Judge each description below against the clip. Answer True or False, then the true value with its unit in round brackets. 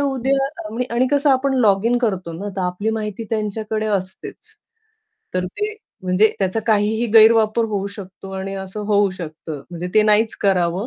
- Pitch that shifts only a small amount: False (3.3 semitones)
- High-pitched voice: True (215 Hz)